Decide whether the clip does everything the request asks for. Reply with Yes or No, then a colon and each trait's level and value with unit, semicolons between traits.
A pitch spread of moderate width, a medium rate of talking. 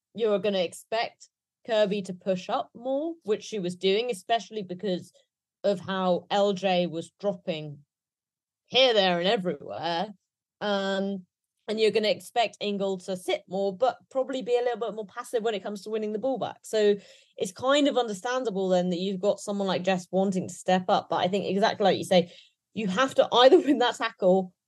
Yes: average, 3.8 semitones; average, 195 wpm